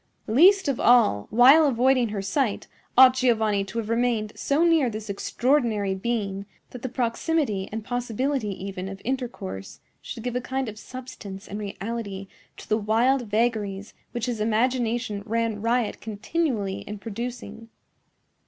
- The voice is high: Yes, high, 230 Hz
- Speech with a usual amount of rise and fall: Yes, average, 3.4 semitones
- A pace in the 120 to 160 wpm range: Yes, average, 145 wpm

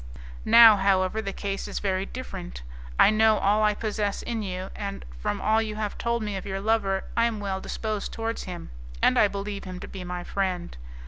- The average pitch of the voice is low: No, high, 200 Hz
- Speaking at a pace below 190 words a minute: No, fast, 205 wpm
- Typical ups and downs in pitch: No, narrow, 2.2 semitones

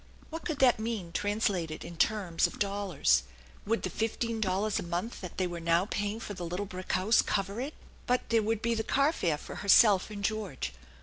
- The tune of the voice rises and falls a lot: No, average, 3.8 semitones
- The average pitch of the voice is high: Yes, high, 205 Hz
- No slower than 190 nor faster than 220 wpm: Yes, fast, 205 wpm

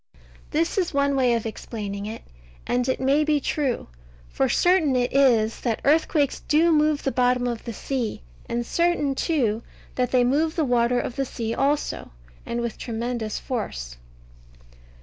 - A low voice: No, very high, 255 Hz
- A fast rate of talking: No, average, 165 wpm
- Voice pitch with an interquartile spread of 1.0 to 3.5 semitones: No, average, 3.9 semitones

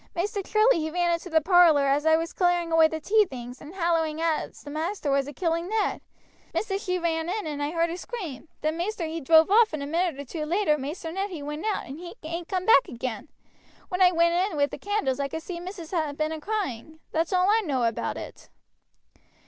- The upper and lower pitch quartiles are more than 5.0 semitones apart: No, average, 3.3 semitones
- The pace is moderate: No, fast, 235 wpm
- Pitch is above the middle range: Yes, very high, 330 Hz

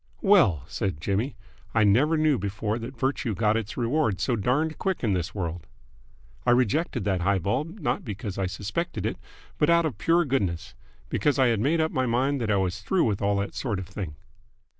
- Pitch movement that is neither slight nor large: No, wide, 6.3 semitones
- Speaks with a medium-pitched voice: No, low, 115 Hz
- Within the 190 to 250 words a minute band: Yes, fast, 205 wpm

